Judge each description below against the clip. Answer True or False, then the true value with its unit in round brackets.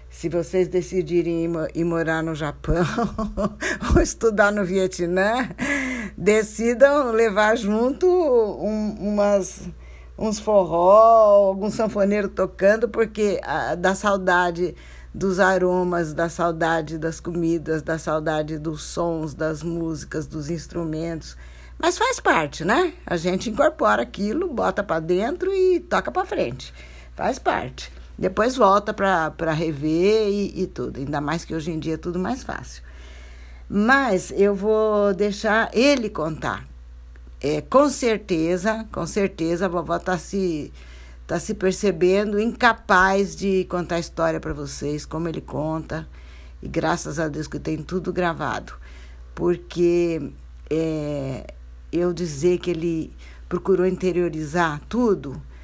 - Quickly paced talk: False (130 wpm)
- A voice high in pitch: False (180 Hz)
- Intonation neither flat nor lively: True (4.5 semitones)